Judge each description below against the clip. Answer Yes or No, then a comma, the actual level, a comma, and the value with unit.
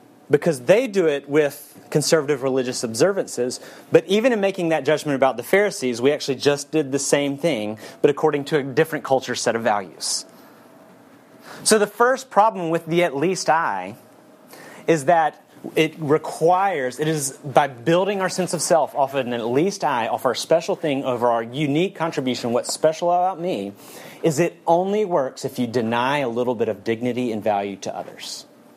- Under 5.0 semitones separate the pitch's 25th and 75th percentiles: No, wide, 5.4 semitones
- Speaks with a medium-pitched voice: Yes, medium, 155 Hz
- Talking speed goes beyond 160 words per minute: Yes, average, 185 wpm